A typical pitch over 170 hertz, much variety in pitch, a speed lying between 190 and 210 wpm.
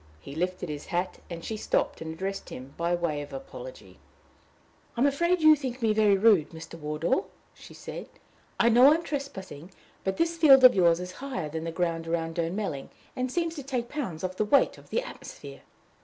Yes: high, 190 Hz; wide, 8.4 semitones; average, 200 wpm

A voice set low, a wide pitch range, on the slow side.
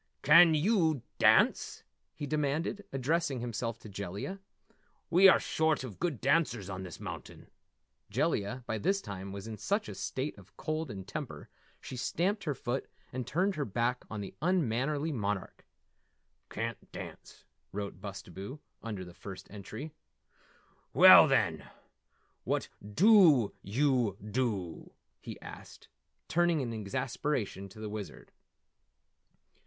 Yes: low, 125 Hz; wide, 7.2 semitones; slow, 130 wpm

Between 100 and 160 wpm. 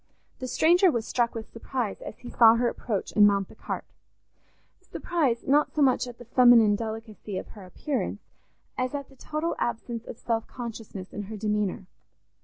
No: average, 175 wpm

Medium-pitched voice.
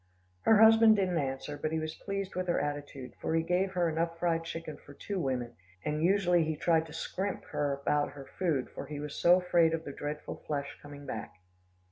Yes: medium, 160 Hz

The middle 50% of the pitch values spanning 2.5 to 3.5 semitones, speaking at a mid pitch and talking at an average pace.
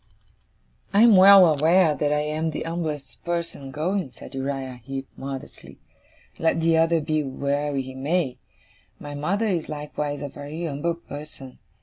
Yes: average, 3.2 semitones; medium, 150 Hz; average, 150 wpm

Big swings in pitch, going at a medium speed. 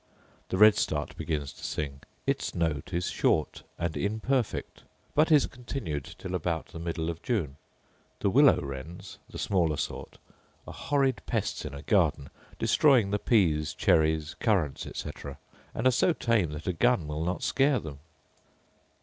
Yes: wide, 7.2 semitones; average, 155 wpm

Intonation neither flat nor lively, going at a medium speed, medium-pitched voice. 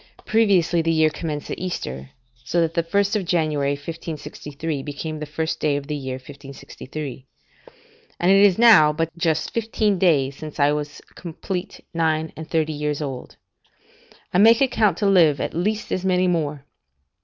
Yes: average, 3.5 semitones; average, 165 wpm; medium, 160 Hz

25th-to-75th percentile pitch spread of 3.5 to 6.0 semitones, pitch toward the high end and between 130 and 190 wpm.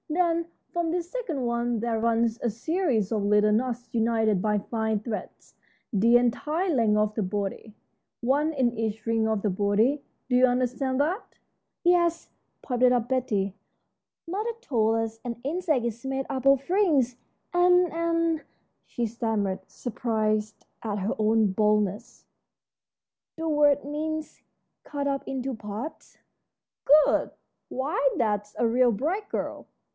Yes: average, 5.3 semitones; high, 240 Hz; average, 140 wpm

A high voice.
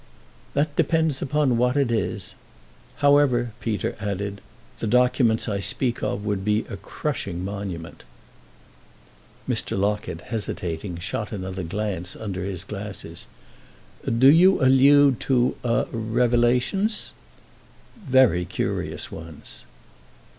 No: low, 110 Hz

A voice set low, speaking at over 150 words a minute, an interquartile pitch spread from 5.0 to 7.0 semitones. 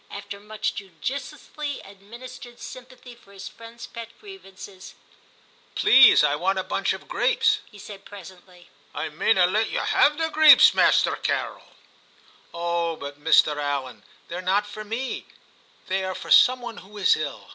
No: high, 205 Hz; average, 165 wpm; wide, 5.4 semitones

